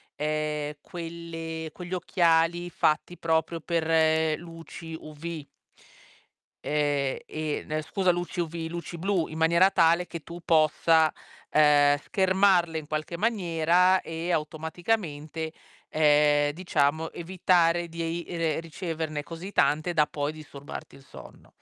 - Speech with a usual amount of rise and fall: No, narrow, 2.0 semitones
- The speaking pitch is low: No, medium, 165 Hz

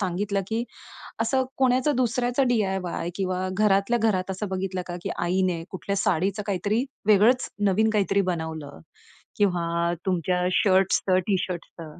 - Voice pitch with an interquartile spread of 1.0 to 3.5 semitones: Yes, average, 2.9 semitones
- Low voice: No, high, 190 Hz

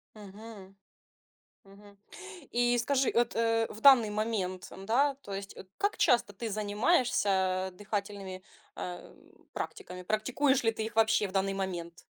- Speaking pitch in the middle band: No, high, 215 Hz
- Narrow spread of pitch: No, average, 3.3 semitones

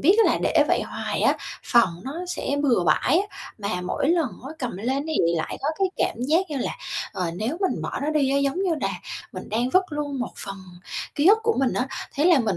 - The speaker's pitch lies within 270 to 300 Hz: Yes, very high, 275 Hz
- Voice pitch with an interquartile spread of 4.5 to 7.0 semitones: Yes, wide, 5.4 semitones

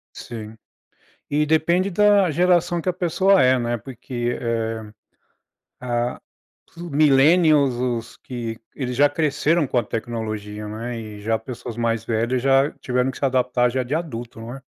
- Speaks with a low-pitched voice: Yes, low, 125 Hz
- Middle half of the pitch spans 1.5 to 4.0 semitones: No, average, 4.7 semitones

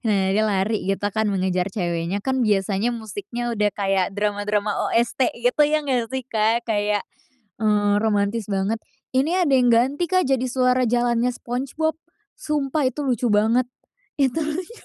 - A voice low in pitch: No, high, 230 Hz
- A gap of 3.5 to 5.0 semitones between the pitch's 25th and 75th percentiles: Yes, average, 4.0 semitones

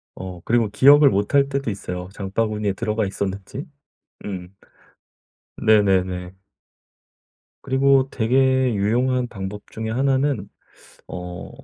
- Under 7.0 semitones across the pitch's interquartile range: Yes, average, 5.2 semitones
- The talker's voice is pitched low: Yes, low, 110 Hz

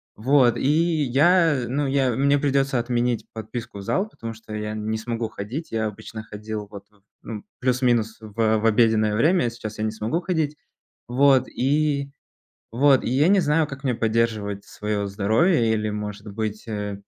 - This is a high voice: No, low, 115 Hz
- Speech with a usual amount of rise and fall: Yes, average, 4.2 semitones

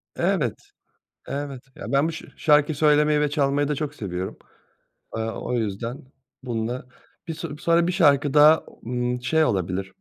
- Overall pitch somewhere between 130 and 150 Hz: Yes, medium, 140 Hz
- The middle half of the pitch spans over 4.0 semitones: No, average, 3.7 semitones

